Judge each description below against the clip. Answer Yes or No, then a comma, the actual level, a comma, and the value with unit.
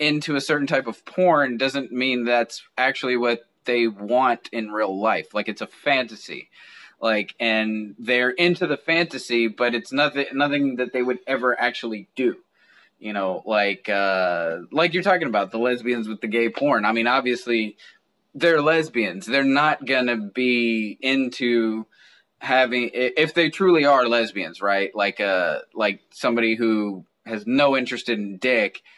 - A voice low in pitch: Yes, low, 120 Hz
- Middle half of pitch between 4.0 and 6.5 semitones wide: No, average, 3.5 semitones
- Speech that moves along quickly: No, average, 160 wpm